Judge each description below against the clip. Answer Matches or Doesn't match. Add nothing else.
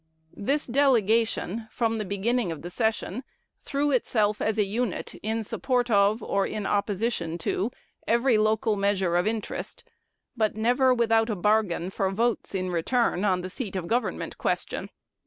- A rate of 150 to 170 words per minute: Matches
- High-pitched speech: Matches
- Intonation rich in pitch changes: Doesn't match